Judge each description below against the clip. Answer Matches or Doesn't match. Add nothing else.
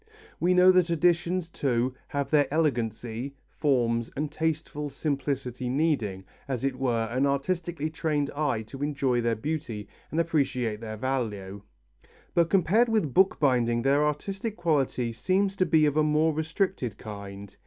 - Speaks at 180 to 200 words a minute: Doesn't match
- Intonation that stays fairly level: Doesn't match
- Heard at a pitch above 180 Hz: Doesn't match